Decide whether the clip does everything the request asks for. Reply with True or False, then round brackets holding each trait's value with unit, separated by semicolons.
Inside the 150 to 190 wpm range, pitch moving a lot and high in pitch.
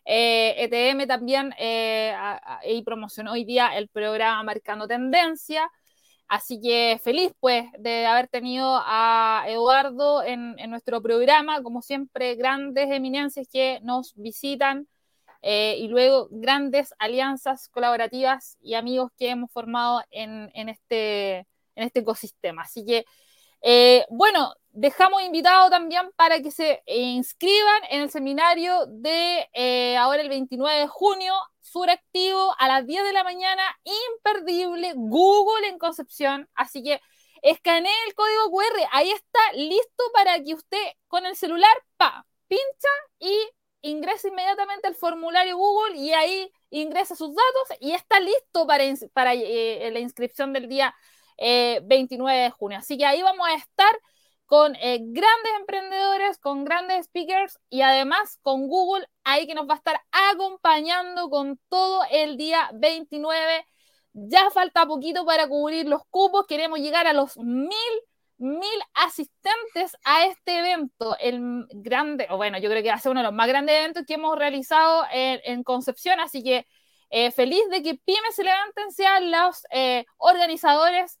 True (155 wpm; 6.5 semitones; 295 Hz)